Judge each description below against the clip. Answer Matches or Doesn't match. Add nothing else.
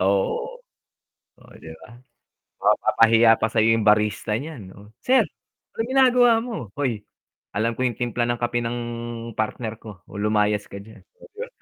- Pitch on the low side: Matches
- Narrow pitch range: Doesn't match